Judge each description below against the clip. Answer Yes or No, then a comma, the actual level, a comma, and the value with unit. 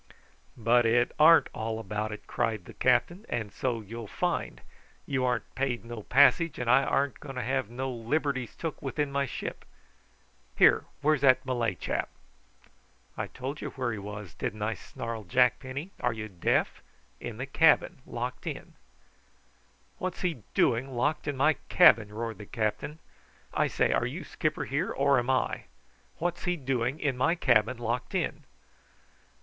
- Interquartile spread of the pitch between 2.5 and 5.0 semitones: Yes, average, 3.5 semitones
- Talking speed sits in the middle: Yes, average, 165 wpm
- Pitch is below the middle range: Yes, low, 125 Hz